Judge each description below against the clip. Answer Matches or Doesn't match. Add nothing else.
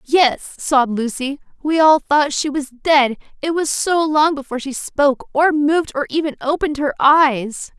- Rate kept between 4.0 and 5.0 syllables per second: Matches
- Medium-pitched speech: Doesn't match